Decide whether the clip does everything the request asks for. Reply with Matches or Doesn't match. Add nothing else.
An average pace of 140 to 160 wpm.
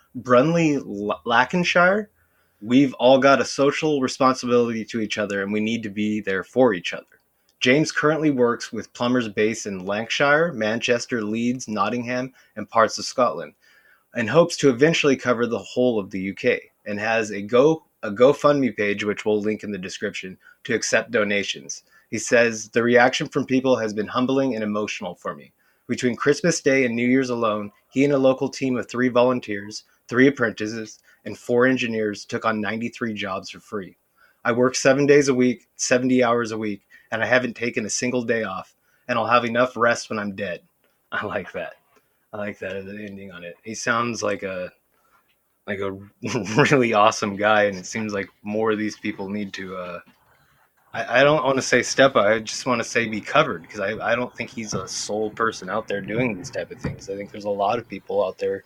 Doesn't match